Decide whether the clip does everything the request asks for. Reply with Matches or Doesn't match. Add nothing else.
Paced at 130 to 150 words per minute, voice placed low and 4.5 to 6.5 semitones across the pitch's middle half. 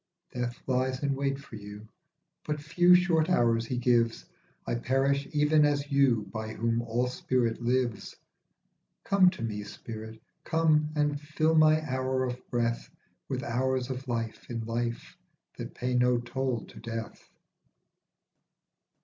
Doesn't match